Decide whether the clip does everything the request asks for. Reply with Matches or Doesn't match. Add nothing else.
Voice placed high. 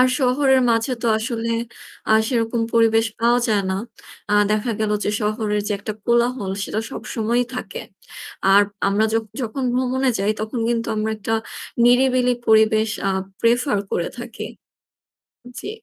Matches